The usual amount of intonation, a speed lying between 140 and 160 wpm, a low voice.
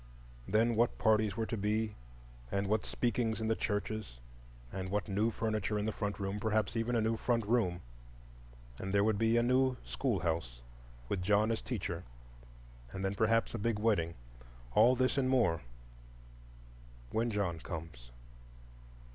Yes: average, 4.3 semitones; average, 145 wpm; low, 105 Hz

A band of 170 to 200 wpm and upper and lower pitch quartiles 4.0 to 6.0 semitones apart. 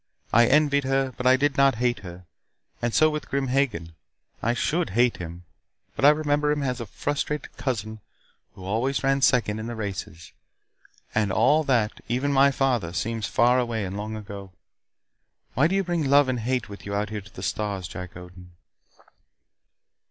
Yes: average, 180 wpm; average, 5.1 semitones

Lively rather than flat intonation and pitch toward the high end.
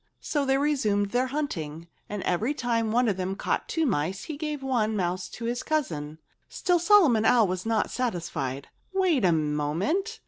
Yes: wide, 8.2 semitones; high, 225 Hz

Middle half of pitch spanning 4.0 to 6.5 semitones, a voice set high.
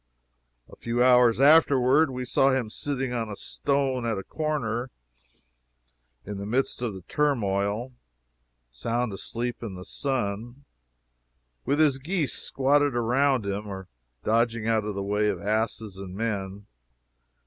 No: average, 4.4 semitones; low, 120 Hz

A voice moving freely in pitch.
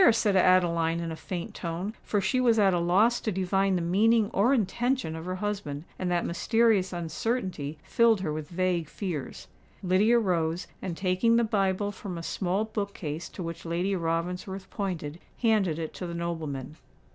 No: average, 3.6 semitones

